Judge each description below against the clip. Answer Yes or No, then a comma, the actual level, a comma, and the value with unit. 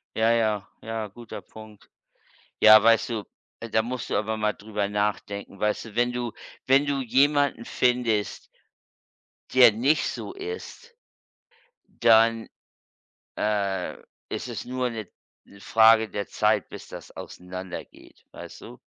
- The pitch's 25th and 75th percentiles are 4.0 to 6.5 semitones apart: No, average, 2.7 semitones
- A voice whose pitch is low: Yes, low, 110 Hz